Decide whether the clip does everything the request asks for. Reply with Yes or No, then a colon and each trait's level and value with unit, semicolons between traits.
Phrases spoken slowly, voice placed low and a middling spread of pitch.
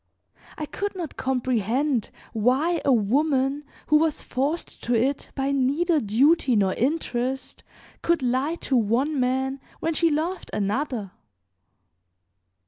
No: slow, 125 wpm; very high, 270 Hz; average, 3.8 semitones